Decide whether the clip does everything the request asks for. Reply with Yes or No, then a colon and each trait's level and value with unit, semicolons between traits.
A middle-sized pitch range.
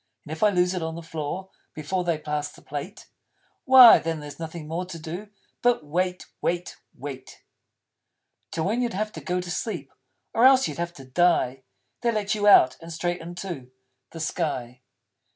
Yes: average, 3.7 semitones